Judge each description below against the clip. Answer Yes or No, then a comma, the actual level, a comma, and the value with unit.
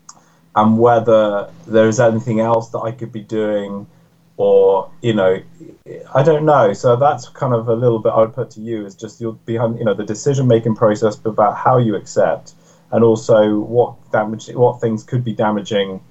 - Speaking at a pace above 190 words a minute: Yes, average, 200 wpm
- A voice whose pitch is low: Yes, low, 115 Hz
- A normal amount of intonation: No, narrow, 1.9 semitones